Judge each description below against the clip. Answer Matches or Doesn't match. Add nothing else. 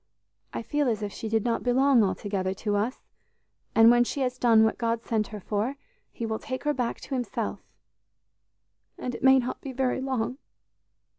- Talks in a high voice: Matches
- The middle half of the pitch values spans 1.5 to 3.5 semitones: Matches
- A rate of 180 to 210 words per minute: Matches